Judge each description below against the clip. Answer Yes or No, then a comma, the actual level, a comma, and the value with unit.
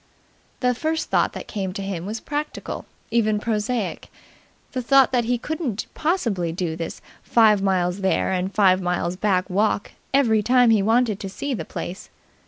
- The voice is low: No, high, 210 Hz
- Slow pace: No, average, 170 wpm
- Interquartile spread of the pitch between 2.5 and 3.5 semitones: No, average, 4.6 semitones